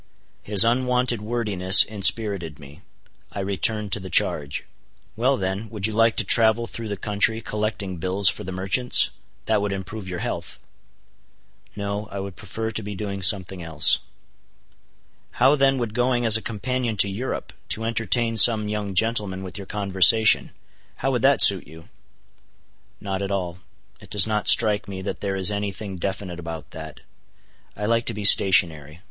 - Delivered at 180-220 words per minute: No, average, 165 wpm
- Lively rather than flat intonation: No, average, 2.9 semitones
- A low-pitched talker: Yes, low, 105 Hz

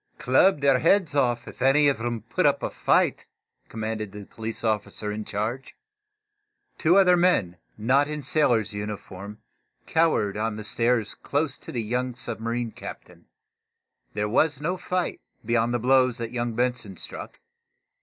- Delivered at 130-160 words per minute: Yes, average, 155 wpm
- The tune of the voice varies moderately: Yes, average, 4.5 semitones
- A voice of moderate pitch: No, low, 120 Hz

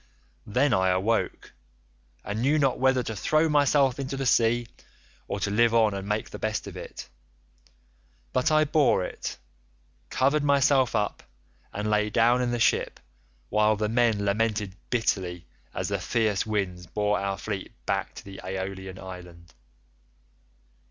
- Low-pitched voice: Yes, low, 110 Hz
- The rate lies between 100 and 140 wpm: No, average, 150 wpm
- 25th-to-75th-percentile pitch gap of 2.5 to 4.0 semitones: No, average, 4.5 semitones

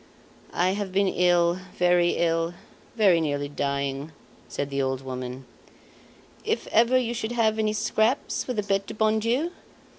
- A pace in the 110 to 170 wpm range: Yes, average, 150 wpm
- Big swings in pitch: Yes, wide, 7.4 semitones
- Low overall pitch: No, medium, 185 Hz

